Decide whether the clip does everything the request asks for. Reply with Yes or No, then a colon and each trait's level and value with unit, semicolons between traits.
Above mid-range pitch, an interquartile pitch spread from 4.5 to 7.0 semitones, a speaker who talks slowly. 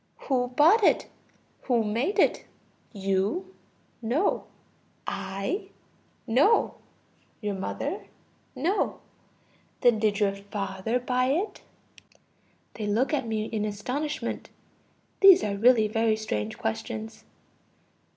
Yes: high, 225 Hz; average, 5.0 semitones; slow, 100 wpm